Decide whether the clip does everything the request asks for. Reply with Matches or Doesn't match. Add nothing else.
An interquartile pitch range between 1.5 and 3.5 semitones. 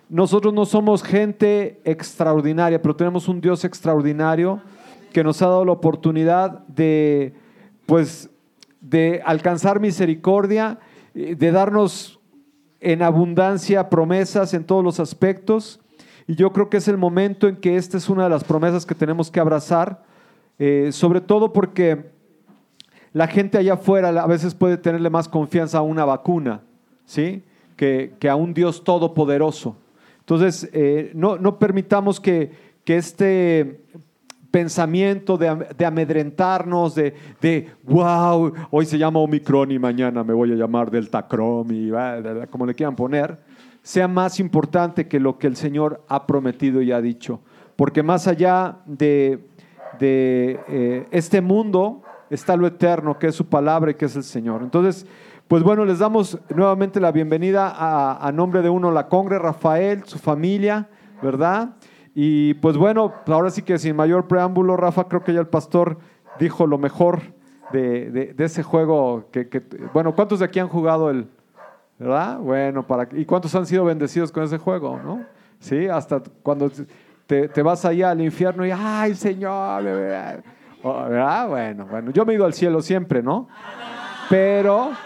Doesn't match